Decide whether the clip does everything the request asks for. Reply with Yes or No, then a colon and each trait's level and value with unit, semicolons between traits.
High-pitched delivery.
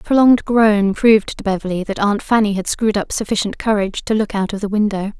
Yes: high, 210 Hz